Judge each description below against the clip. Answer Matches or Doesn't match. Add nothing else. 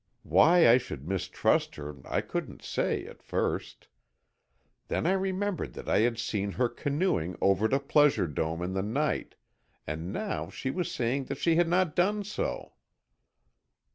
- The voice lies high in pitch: Doesn't match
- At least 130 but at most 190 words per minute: Matches